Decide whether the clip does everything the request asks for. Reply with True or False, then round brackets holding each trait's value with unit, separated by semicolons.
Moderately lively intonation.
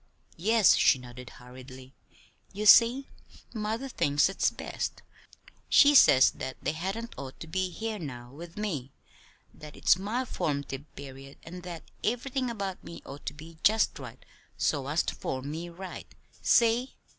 False (7.9 semitones)